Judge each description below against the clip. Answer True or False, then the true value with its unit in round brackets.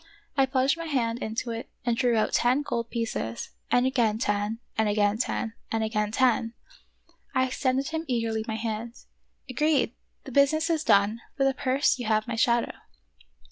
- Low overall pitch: False (235 Hz)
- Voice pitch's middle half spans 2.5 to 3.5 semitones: True (3.1 semitones)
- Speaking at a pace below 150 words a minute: False (175 wpm)